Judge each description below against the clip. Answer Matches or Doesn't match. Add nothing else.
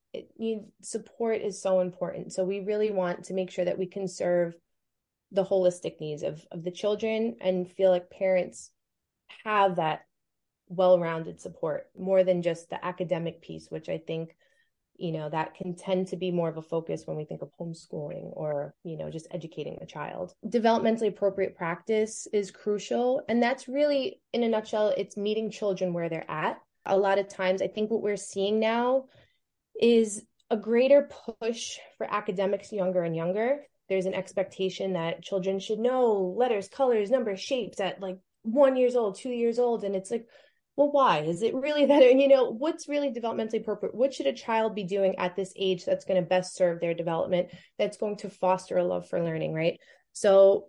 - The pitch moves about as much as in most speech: Matches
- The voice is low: Doesn't match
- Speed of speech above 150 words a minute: Matches